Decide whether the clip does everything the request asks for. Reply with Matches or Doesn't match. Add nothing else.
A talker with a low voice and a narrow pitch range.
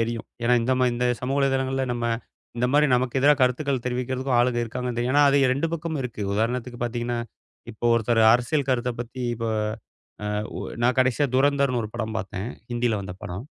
Matches